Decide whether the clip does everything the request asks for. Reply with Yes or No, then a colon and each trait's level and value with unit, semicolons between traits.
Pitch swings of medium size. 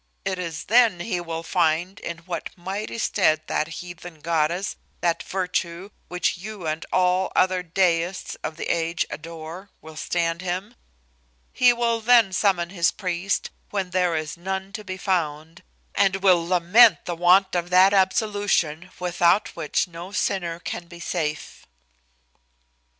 No: narrow, 2.3 semitones